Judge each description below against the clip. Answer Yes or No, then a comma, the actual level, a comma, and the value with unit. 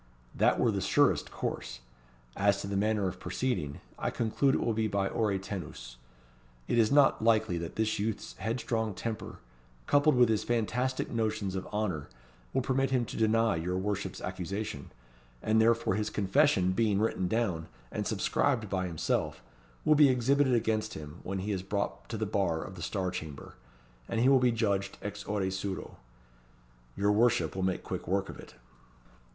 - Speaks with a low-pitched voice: Yes, low, 105 Hz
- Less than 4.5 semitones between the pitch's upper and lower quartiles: Yes, average, 3.5 semitones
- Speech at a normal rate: Yes, average, 175 wpm